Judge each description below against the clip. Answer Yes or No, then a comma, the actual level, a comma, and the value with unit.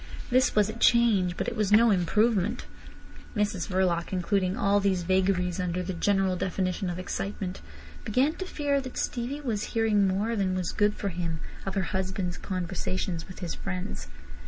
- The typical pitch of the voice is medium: No, high, 195 Hz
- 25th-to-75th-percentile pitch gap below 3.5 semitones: Yes, average, 2.9 semitones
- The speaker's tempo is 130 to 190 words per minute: Yes, average, 170 wpm